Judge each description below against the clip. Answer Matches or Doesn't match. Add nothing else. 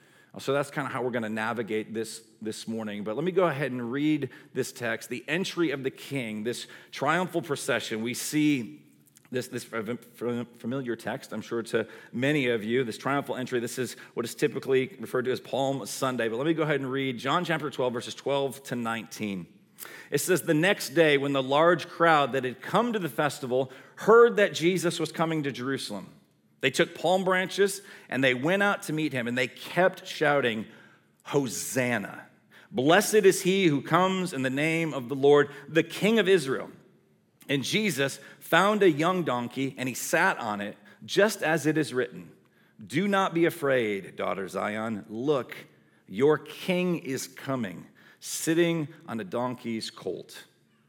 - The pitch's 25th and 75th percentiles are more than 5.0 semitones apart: Matches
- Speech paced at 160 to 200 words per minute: Matches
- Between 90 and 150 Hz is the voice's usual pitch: Matches